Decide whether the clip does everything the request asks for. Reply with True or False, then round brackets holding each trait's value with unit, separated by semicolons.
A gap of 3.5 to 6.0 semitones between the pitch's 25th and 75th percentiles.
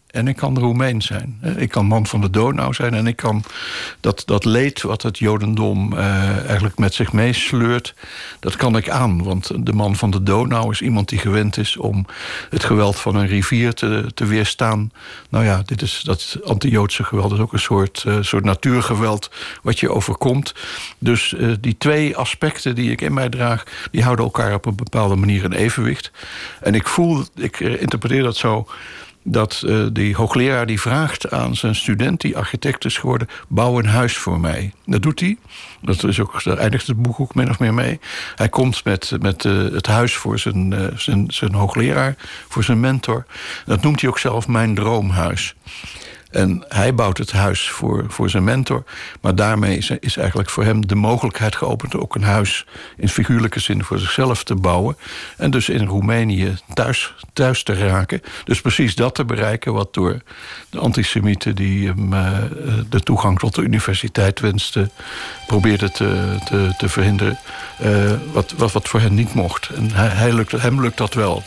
False (3.1 semitones)